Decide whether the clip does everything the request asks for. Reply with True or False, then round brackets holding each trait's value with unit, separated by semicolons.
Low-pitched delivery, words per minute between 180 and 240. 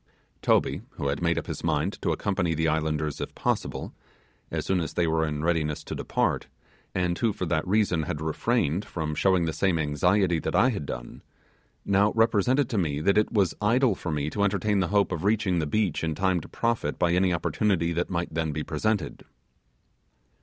True (85 Hz; 200 wpm)